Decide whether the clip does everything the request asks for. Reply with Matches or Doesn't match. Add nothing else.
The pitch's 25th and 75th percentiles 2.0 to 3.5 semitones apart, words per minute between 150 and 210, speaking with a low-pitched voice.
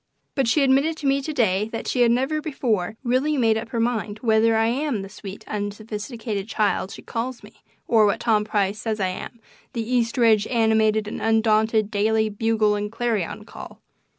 Doesn't match